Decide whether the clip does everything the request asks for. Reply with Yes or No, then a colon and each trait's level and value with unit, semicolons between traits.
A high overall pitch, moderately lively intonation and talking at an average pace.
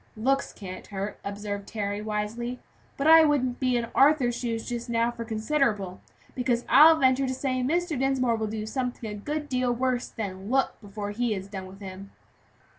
Yes: high, 235 Hz; average, 3.9 semitones; average, 185 wpm